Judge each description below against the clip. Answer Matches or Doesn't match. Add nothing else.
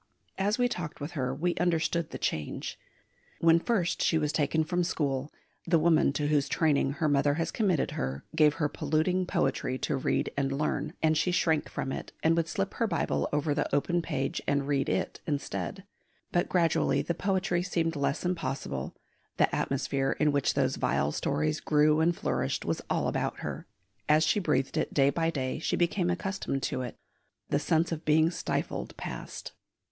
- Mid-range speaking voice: Matches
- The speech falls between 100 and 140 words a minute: Doesn't match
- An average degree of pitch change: Matches